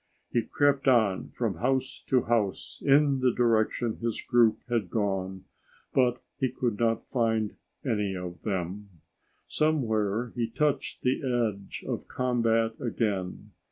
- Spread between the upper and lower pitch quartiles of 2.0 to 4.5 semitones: Yes, average, 3.4 semitones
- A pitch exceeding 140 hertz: No, low, 115 Hz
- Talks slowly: Yes, slow, 130 wpm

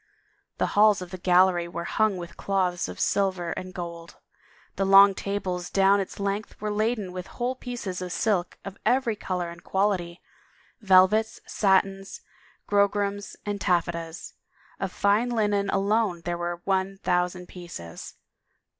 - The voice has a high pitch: Yes, high, 195 Hz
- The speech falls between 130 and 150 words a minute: Yes, average, 145 wpm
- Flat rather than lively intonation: Yes, narrow, 2.3 semitones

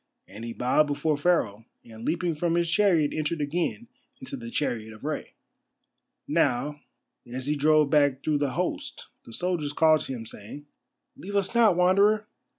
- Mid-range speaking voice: Yes, medium, 150 Hz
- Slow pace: No, average, 165 wpm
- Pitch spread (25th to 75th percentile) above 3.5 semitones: Yes, average, 5.2 semitones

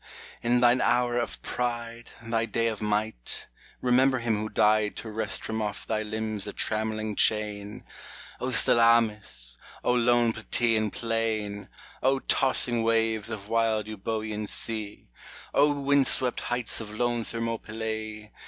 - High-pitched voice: No, low, 110 Hz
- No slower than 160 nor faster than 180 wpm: No, slow, 135 wpm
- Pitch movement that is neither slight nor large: No, narrow, 1.7 semitones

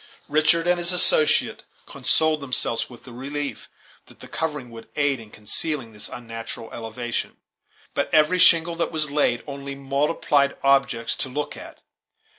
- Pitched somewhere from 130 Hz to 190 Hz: Yes, medium, 140 Hz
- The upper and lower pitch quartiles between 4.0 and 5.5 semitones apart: Yes, average, 4.6 semitones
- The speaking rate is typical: Yes, average, 150 wpm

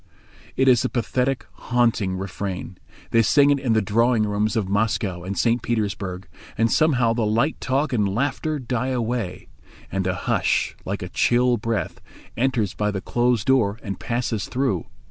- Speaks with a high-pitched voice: No, low, 115 Hz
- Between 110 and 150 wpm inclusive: No, average, 165 wpm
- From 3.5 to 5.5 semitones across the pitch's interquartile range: Yes, average, 3.9 semitones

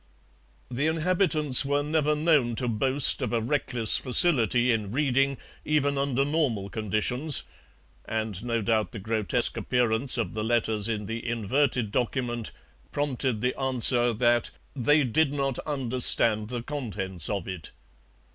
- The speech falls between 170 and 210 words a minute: No, slow, 135 wpm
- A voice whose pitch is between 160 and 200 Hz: No, low, 125 Hz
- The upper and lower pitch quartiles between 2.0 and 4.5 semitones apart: Yes, average, 4.0 semitones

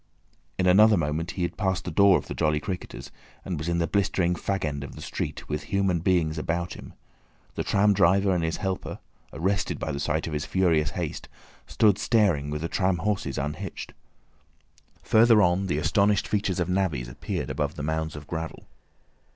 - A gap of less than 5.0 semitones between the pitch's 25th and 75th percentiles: Yes, average, 3.8 semitones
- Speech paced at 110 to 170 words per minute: No, average, 185 wpm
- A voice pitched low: Yes, very low, 90 Hz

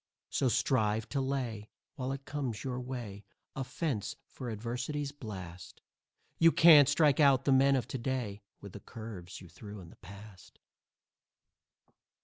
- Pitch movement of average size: Yes, average, 4.7 semitones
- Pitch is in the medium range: No, low, 125 Hz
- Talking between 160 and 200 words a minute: No, average, 150 wpm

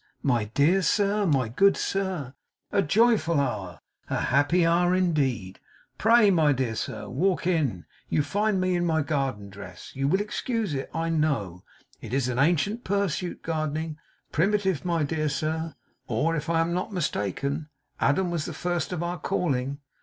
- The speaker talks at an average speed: Yes, average, 165 wpm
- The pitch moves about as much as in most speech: Yes, average, 4.8 semitones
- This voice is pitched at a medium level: Yes, medium, 160 Hz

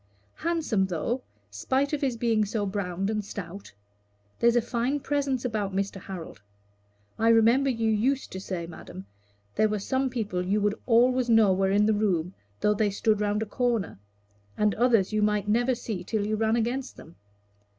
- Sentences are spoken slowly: No, average, 180 wpm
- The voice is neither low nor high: No, high, 215 Hz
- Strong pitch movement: No, average, 3.4 semitones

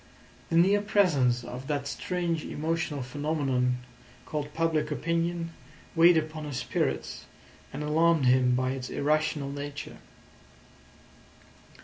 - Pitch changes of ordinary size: Yes, average, 3.8 semitones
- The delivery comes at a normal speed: No, slow, 110 wpm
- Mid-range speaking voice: Yes, medium, 150 Hz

